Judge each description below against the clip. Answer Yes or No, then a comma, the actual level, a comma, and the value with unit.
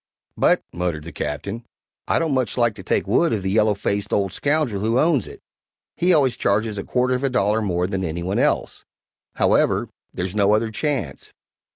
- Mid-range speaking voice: No, low, 105 Hz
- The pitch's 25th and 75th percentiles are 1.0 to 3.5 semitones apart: No, average, 4.8 semitones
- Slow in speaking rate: No, average, 195 wpm